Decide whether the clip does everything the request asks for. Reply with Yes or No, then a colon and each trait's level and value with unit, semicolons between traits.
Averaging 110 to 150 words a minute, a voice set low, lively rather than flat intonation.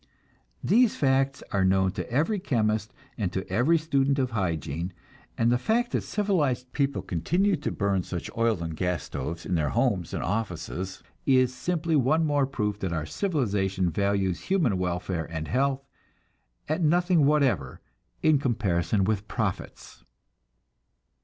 Yes: average, 145 wpm; low, 115 Hz; wide, 7.5 semitones